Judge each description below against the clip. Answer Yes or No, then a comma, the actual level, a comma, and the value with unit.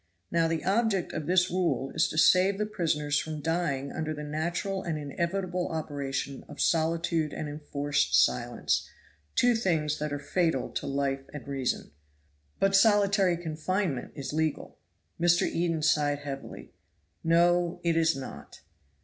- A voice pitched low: No, medium, 160 Hz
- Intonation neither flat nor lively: Yes, average, 3.4 semitones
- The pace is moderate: Yes, average, 145 wpm